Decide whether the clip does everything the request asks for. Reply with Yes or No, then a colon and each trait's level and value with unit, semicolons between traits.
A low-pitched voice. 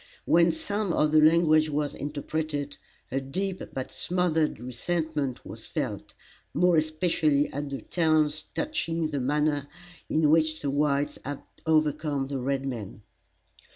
No: medium, 150 Hz